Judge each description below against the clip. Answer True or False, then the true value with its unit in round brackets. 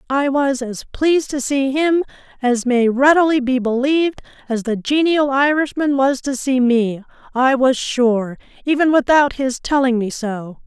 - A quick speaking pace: False (165 wpm)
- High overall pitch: True (265 Hz)